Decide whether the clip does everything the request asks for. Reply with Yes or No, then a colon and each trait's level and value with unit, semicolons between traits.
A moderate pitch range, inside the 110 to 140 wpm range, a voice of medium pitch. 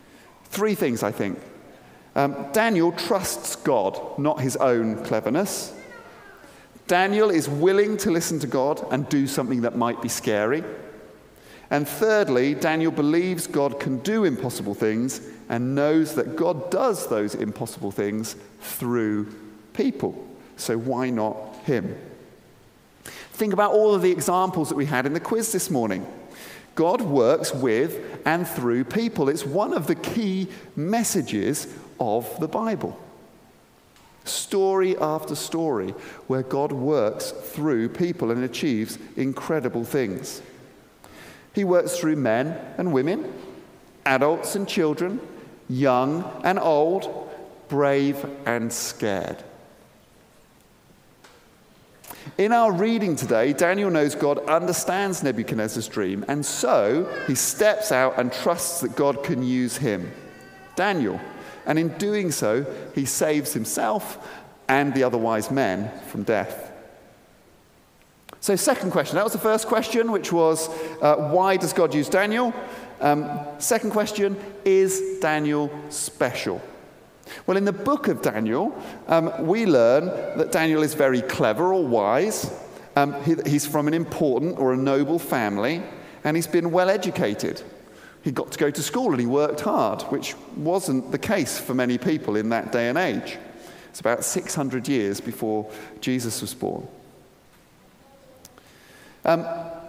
No: wide, 6.3 semitones; slow, 135 wpm; medium, 150 Hz